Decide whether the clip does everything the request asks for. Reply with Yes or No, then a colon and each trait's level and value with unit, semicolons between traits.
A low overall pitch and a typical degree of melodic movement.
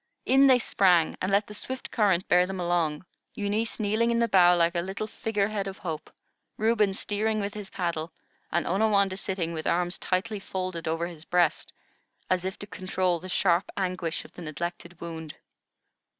No: medium, 185 Hz; average, 3.2 semitones